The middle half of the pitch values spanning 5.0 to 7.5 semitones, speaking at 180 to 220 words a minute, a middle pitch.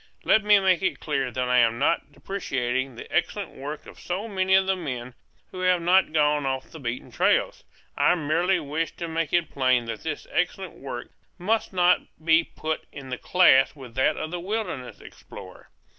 Yes: wide, 5.6 semitones; average, 190 wpm; medium, 160 Hz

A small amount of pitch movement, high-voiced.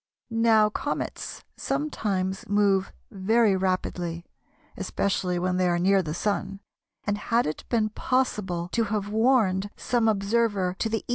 No: average, 3.2 semitones; high, 200 Hz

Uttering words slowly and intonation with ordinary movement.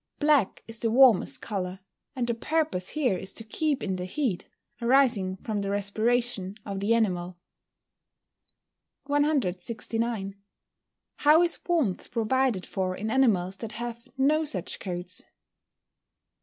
No: slow, 130 wpm; wide, 5.7 semitones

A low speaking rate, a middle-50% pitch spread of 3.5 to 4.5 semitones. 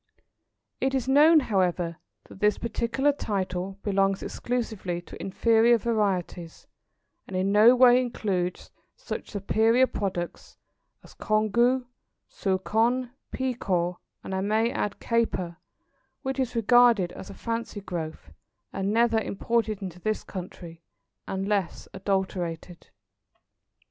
Yes: slow, 115 wpm; average, 4.0 semitones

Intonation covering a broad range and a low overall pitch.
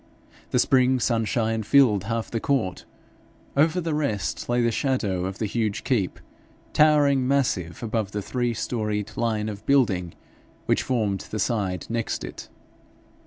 No: average, 4.1 semitones; low, 115 Hz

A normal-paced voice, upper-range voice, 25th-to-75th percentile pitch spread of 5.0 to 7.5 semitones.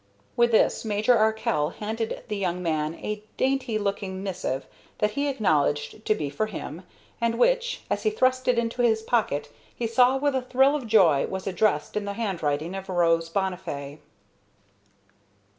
Yes: average, 165 wpm; high, 210 Hz; wide, 5.5 semitones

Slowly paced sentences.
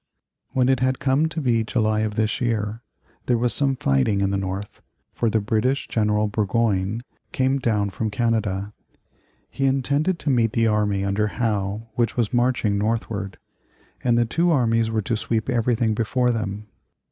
No: average, 170 wpm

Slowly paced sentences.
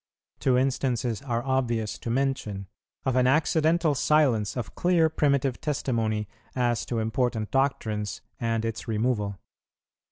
Yes: slow, 125 wpm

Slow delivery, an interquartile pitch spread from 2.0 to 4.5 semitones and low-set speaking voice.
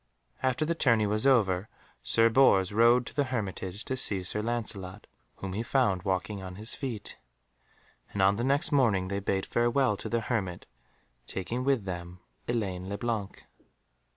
No: average, 165 wpm; average, 4.0 semitones; low, 105 Hz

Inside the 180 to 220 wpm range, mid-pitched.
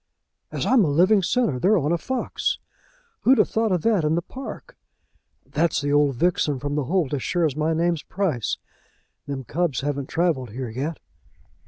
Yes: average, 185 wpm; medium, 160 Hz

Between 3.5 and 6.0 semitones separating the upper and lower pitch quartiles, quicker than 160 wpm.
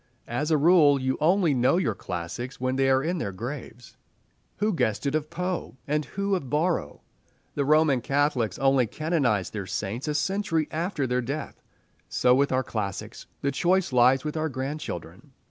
Yes: average, 4.2 semitones; average, 175 wpm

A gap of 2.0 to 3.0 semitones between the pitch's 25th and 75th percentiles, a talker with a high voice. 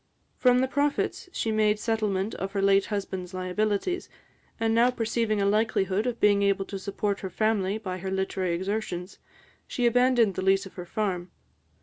Yes: average, 2.7 semitones; high, 205 Hz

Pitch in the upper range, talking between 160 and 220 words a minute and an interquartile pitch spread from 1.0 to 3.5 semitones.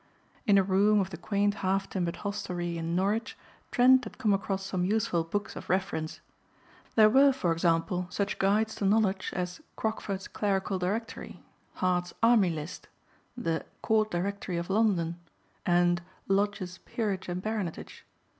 No: high, 195 Hz; average, 145 wpm; average, 3.0 semitones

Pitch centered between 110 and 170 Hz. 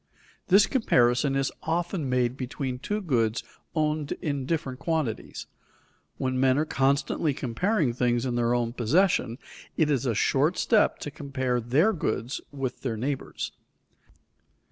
Yes: low, 135 Hz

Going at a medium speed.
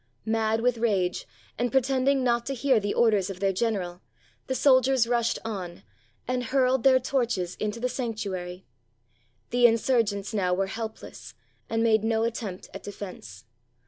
Yes: average, 150 wpm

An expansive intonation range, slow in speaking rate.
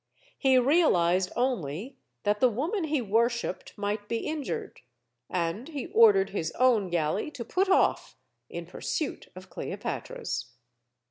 Yes: wide, 7.9 semitones; slow, 130 wpm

